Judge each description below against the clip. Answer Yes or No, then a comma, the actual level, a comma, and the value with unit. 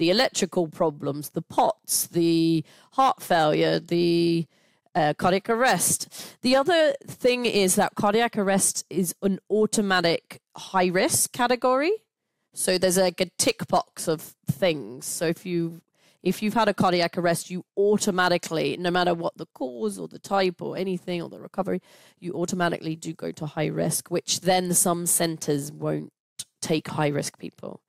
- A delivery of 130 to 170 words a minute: Yes, average, 155 wpm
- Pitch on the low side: No, medium, 180 Hz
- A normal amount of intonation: Yes, average, 3.0 semitones